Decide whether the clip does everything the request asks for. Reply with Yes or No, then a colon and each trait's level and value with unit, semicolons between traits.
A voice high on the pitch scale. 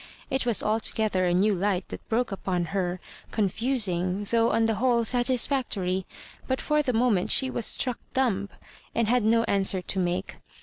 Yes: high, 220 Hz